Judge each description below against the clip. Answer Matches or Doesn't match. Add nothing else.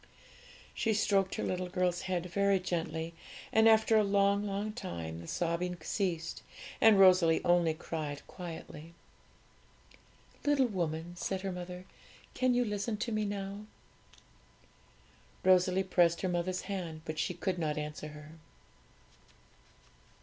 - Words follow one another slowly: Matches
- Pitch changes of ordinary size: Matches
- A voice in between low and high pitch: Matches